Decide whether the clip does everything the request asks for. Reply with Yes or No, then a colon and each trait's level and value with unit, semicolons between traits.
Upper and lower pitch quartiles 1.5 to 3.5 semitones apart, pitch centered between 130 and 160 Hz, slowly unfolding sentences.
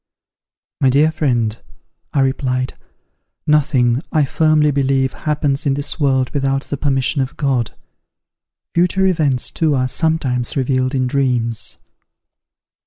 Yes: average, 2.7 semitones; low, 135 Hz; slow, 120 wpm